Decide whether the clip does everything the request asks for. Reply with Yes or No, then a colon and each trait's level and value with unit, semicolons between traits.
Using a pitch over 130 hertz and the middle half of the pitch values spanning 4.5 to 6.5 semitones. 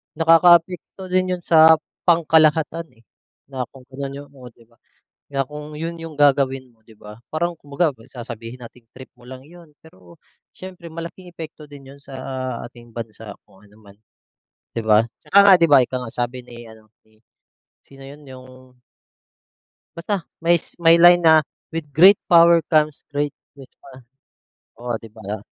Yes: medium, 140 Hz; average, 5.2 semitones